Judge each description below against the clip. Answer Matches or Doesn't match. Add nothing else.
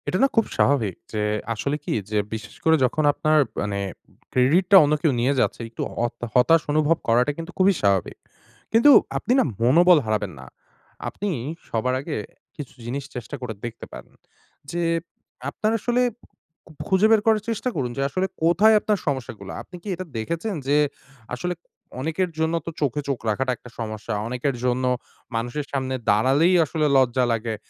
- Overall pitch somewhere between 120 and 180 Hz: Matches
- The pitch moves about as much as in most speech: Doesn't match